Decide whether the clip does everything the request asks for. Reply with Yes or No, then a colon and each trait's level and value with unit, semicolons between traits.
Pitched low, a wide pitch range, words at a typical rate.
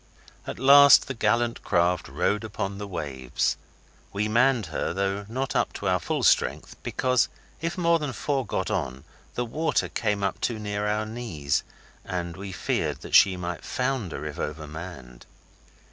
Yes: low, 105 Hz; wide, 6.1 semitones; average, 160 wpm